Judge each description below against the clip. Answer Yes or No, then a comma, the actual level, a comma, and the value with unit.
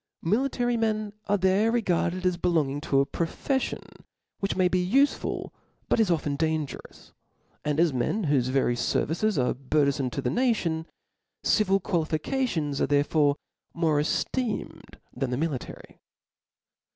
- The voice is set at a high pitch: No, medium, 165 Hz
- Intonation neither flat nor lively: No, wide, 6.3 semitones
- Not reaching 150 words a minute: Yes, average, 140 wpm